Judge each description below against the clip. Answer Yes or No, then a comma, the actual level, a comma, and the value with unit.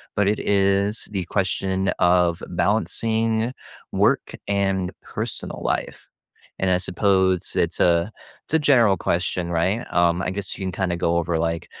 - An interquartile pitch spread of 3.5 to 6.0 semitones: No, narrow, 2.4 semitones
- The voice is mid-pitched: No, very low, 95 Hz